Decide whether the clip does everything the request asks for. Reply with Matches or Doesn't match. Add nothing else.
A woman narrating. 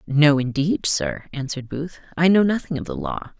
Matches